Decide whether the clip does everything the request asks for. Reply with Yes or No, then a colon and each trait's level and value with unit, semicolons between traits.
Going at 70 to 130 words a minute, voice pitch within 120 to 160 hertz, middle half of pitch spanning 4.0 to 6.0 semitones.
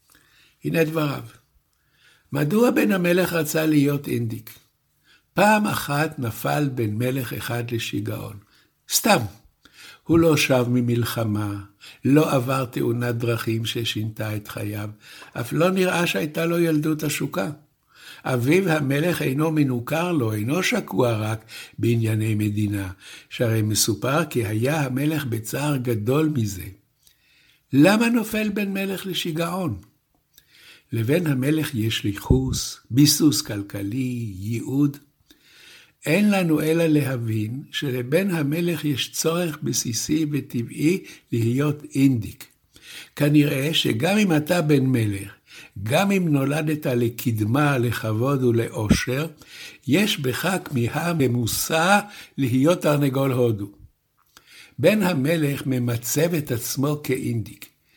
Yes: average, 105 wpm; low, 135 Hz; average, 5.0 semitones